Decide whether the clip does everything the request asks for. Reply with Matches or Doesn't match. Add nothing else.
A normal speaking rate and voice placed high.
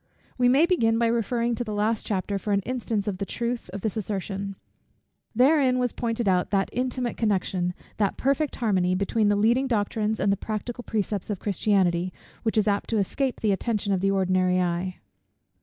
Matches